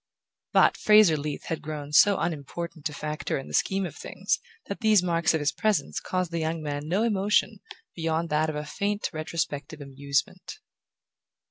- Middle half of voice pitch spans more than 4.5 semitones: No, average, 4.2 semitones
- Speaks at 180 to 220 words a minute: No, average, 170 wpm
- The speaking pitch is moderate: Yes, medium, 160 Hz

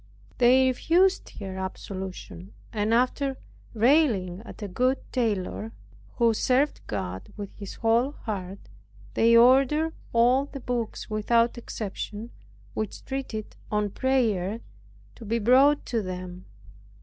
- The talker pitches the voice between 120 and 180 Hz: No, high, 230 Hz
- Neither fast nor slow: No, slow, 120 wpm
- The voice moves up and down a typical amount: Yes, average, 4.3 semitones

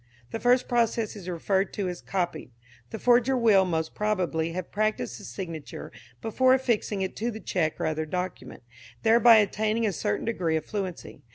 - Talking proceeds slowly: No, average, 175 wpm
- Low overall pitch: No, high, 200 Hz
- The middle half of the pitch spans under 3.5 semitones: No, average, 4.7 semitones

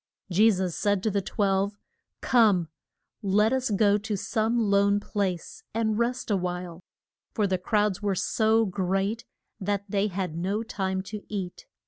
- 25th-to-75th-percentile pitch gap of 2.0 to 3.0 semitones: Yes, narrow, 2.4 semitones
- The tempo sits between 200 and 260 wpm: No, average, 155 wpm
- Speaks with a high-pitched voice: Yes, high, 200 Hz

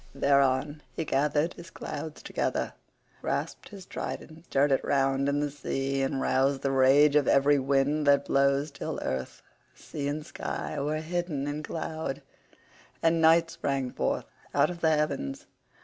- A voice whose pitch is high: No, medium, 145 Hz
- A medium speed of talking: Yes, average, 155 wpm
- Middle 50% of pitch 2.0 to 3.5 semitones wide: Yes, narrow, 2.5 semitones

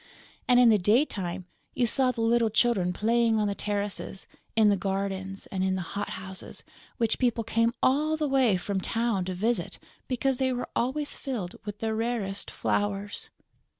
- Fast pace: No, average, 175 wpm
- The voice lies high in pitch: Yes, high, 220 Hz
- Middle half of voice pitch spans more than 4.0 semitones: No, average, 3.7 semitones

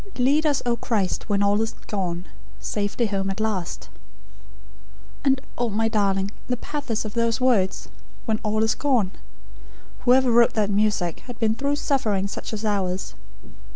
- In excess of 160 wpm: No, average, 155 wpm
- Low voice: No, high, 220 Hz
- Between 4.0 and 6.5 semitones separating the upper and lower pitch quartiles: No, average, 3.4 semitones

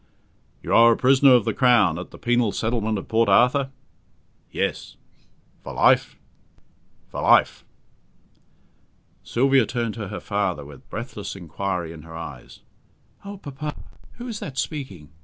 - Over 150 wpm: No, average, 140 wpm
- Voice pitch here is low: Yes, low, 115 Hz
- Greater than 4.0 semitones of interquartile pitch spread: Yes, average, 5.3 semitones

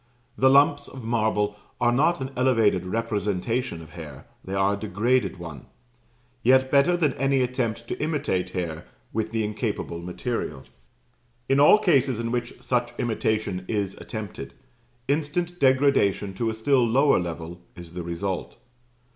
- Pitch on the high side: No, low, 115 Hz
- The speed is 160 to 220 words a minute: No, average, 145 wpm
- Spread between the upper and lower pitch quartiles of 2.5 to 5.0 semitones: No, wide, 5.6 semitones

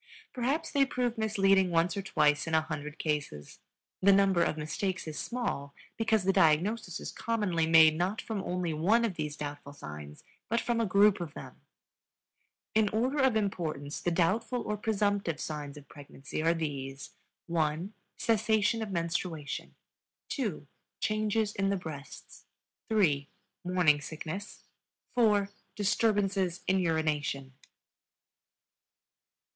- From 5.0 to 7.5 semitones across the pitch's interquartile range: Yes, wide, 5.5 semitones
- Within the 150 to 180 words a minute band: No, slow, 135 wpm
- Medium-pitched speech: Yes, medium, 180 Hz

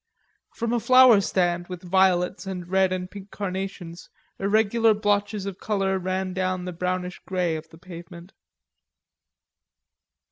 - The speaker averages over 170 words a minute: No, average, 140 wpm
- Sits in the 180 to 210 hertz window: Yes, medium, 185 Hz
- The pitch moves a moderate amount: No, narrow, 1.9 semitones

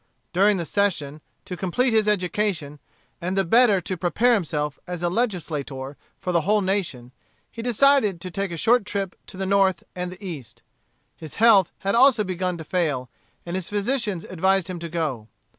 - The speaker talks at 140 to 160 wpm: No, average, 180 wpm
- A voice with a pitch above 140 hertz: Yes, medium, 185 Hz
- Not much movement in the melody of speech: No, average, 3.8 semitones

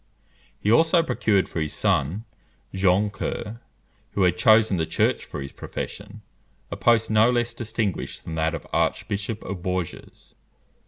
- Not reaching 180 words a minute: Yes, average, 150 wpm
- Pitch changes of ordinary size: Yes, average, 3.9 semitones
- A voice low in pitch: Yes, low, 100 Hz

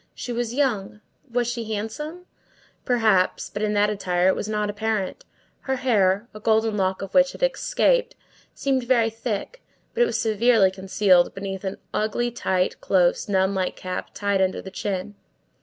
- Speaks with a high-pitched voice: Yes, high, 210 Hz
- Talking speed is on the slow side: No, average, 165 wpm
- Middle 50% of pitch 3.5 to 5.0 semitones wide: Yes, average, 3.8 semitones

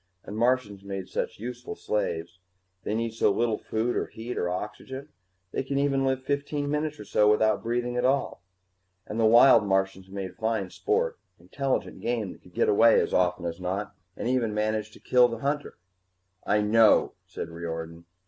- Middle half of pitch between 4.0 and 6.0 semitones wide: Yes, average, 4.6 semitones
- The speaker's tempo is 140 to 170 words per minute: No, average, 180 wpm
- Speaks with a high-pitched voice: No, low, 110 Hz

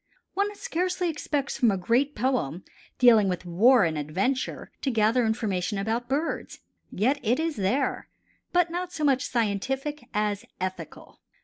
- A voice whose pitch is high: Yes, high, 245 Hz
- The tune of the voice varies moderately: No, wide, 6.2 semitones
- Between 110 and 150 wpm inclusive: Yes, average, 145 wpm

